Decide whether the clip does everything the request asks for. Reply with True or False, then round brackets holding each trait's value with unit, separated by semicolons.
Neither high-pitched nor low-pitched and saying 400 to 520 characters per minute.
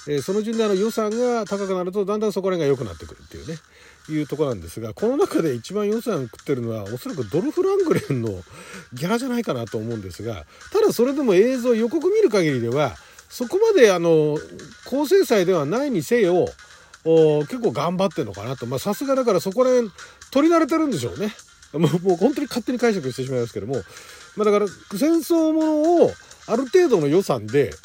False (200 Hz; 415 characters per minute)